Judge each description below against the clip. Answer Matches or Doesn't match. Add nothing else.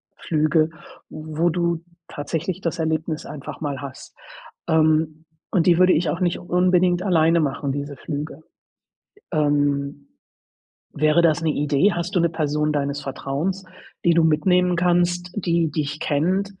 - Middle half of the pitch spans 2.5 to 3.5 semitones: Matches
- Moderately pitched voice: Matches